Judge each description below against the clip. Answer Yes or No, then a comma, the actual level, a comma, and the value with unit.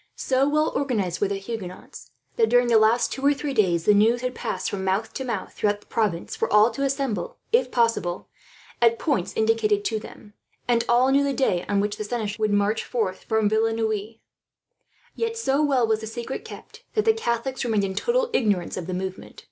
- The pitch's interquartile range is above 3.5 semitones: Yes, average, 4.1 semitones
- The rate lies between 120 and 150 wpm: No, fast, 205 wpm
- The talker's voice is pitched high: Yes, high, 225 Hz